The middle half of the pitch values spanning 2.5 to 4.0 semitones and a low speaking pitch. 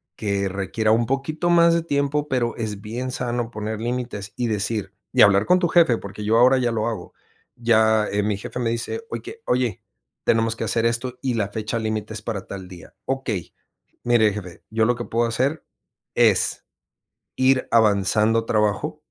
Yes: average, 2.9 semitones; low, 115 Hz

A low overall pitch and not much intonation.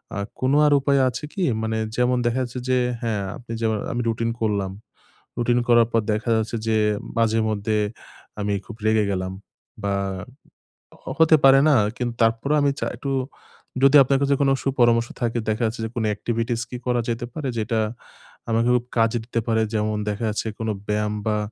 Yes: low, 115 Hz; narrow, 2.1 semitones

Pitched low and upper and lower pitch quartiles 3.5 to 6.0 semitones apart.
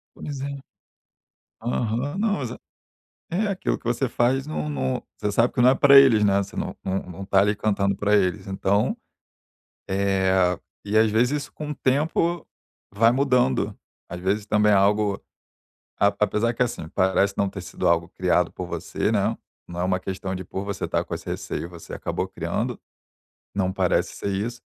Yes: low, 105 Hz; average, 4.7 semitones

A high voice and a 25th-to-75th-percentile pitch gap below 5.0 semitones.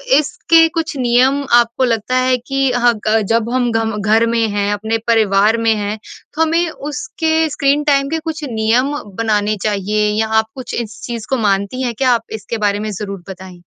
Yes: high, 230 Hz; average, 4.3 semitones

